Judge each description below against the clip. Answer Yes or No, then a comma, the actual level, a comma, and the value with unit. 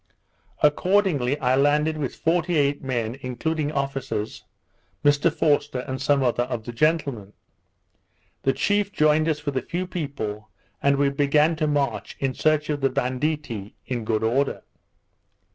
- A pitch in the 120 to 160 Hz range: Yes, medium, 140 Hz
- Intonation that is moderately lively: Yes, average, 3.2 semitones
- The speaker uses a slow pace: No, average, 145 wpm